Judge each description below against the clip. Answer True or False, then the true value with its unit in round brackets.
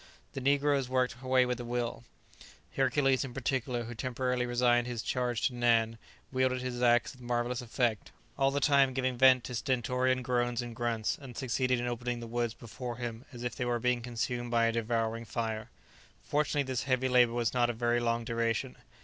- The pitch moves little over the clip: True (1.5 semitones)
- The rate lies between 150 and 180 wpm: False (190 wpm)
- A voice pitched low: True (120 Hz)